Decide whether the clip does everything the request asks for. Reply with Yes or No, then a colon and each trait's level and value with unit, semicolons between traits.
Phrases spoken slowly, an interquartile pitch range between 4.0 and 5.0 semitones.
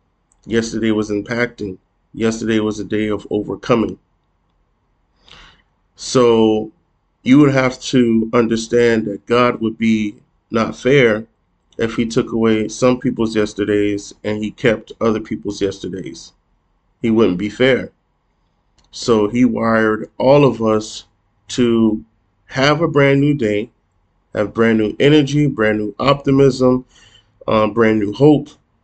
No: slow, 125 wpm; average, 2.9 semitones